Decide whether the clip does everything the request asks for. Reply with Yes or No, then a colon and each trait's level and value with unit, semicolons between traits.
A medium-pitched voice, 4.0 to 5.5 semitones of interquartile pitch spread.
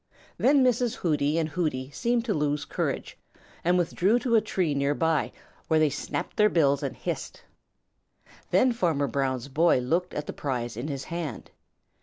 Yes: medium, 155 Hz; average, 4.7 semitones